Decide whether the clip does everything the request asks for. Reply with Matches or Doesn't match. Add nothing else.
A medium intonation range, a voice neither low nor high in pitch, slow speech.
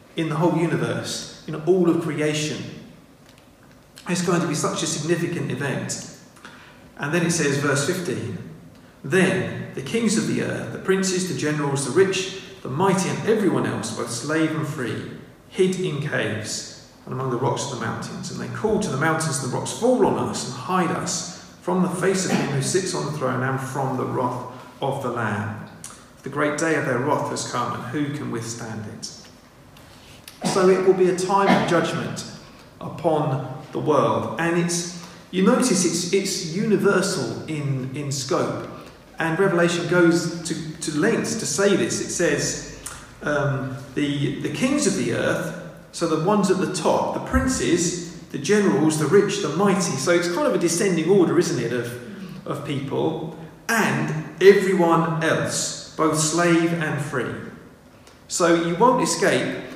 Doesn't match